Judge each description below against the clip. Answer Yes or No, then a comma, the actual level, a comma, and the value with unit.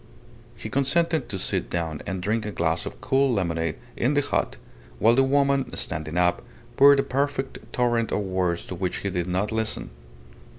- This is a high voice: No, low, 105 Hz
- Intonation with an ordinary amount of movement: No, wide, 7.2 semitones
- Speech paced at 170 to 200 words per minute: Yes, average, 180 wpm